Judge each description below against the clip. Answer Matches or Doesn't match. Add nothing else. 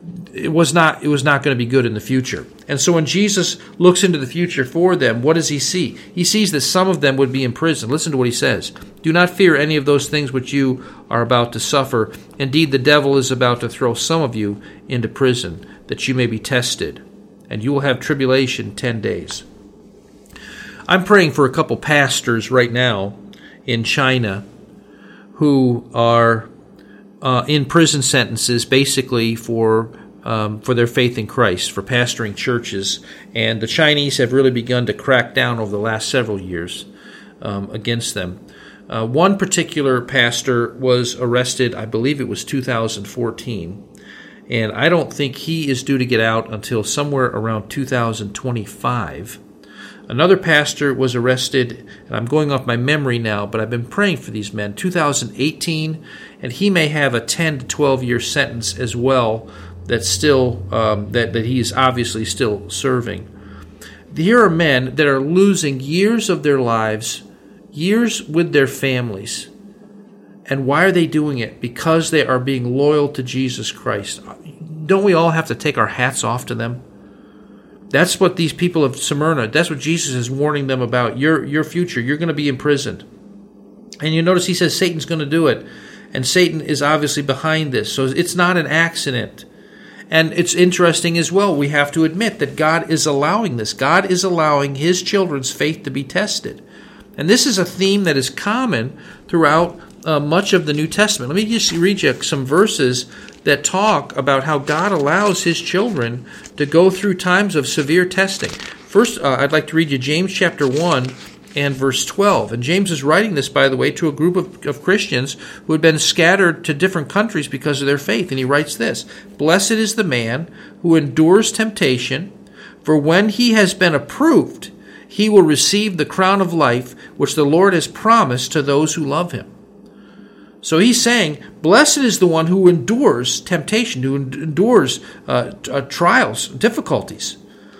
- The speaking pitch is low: Doesn't match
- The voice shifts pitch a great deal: Matches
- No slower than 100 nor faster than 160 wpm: Doesn't match